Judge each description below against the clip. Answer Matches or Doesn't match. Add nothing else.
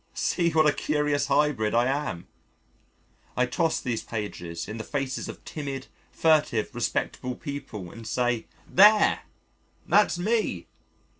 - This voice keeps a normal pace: Doesn't match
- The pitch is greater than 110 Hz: Matches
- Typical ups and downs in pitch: Matches